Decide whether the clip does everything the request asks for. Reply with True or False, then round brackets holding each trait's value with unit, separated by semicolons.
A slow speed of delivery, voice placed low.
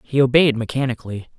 True (130 wpm; 125 Hz)